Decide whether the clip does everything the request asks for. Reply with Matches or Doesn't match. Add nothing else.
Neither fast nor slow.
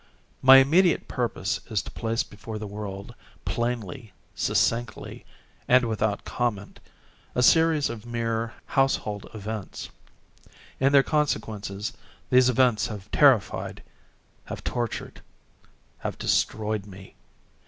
Doesn't match